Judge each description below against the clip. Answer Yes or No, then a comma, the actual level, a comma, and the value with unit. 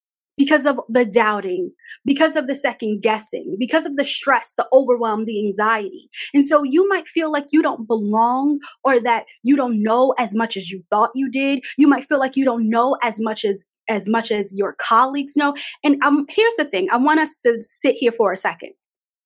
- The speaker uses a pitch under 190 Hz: No, very high, 260 Hz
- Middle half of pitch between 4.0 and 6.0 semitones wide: Yes, average, 4.3 semitones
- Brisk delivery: Yes, fast, 210 wpm